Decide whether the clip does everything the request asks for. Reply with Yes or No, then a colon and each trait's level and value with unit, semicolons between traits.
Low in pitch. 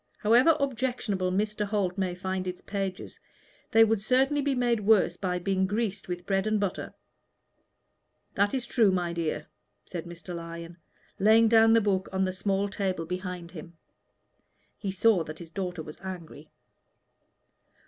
No: high, 195 Hz